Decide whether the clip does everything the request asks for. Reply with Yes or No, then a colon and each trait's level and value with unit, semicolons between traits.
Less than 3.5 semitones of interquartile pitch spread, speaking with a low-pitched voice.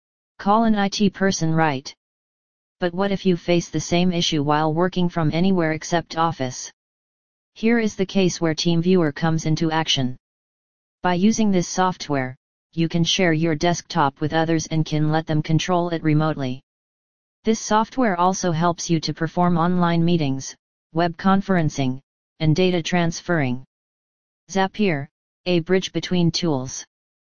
No: narrow, 2.6 semitones; medium, 170 Hz